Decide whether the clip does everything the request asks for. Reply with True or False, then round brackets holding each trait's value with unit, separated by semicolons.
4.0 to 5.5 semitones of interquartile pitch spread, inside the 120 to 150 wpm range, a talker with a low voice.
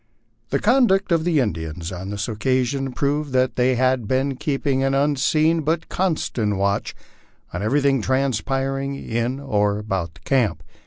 True (4.9 semitones; 145 wpm; 130 Hz)